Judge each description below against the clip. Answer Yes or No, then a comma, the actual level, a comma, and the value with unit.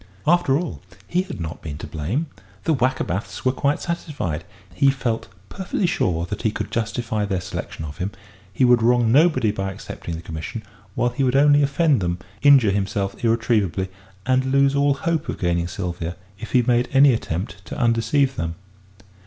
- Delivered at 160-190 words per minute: Yes, average, 180 wpm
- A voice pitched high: No, low, 115 Hz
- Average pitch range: No, wide, 6.7 semitones